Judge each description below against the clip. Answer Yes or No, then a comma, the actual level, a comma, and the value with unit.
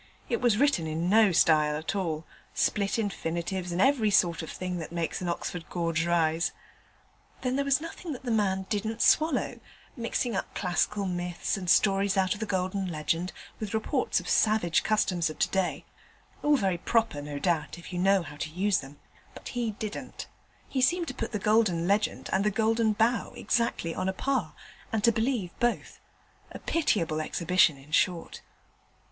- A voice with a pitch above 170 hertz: Yes, high, 190 Hz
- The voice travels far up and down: No, average, 4.5 semitones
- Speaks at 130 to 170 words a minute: No, average, 180 wpm